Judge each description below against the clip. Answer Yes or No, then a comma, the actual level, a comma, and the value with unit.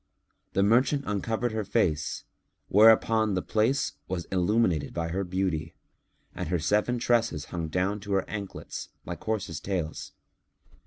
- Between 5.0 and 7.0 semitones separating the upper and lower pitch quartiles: No, average, 4.1 semitones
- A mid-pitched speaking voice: No, low, 100 Hz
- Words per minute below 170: Yes, average, 140 wpm